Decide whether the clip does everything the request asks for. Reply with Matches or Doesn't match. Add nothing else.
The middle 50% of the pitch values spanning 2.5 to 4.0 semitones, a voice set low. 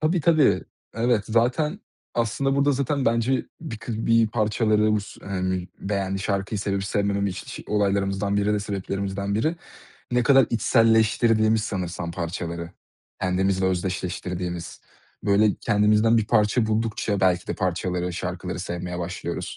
Matches